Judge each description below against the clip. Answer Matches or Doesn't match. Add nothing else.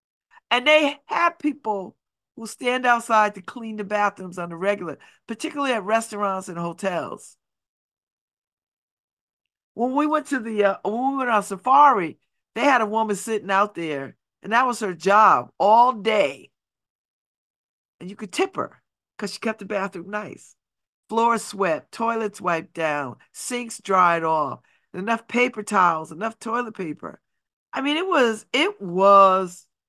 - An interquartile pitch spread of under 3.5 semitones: Doesn't match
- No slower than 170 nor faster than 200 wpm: Doesn't match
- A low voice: Doesn't match